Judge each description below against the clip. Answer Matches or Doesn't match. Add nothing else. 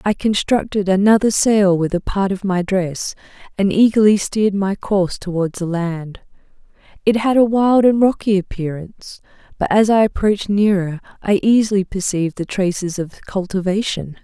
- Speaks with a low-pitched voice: Doesn't match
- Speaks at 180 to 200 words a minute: Doesn't match